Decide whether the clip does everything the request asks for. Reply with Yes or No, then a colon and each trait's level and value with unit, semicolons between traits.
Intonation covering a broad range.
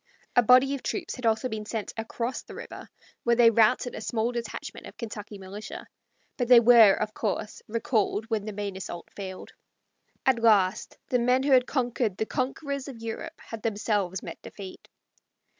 No: average, 2.9 semitones